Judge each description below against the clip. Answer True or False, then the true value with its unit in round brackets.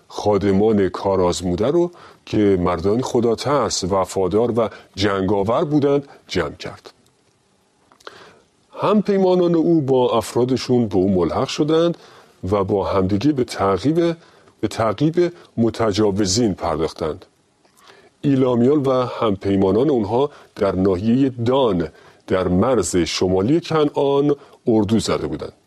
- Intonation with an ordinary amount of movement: False (6.6 semitones)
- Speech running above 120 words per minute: False (105 wpm)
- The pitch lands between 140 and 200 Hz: False (120 Hz)